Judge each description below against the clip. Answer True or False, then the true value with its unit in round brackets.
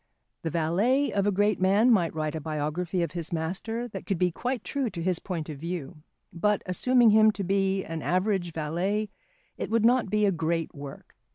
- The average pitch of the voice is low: False (185 Hz)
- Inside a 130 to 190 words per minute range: False (200 wpm)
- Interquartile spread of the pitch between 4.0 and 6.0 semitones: True (4.4 semitones)